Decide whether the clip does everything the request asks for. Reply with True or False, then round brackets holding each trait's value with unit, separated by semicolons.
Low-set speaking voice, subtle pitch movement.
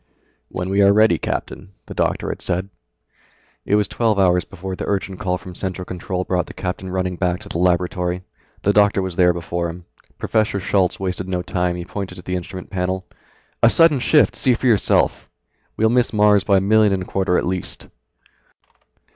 True (95 Hz; 2.1 semitones)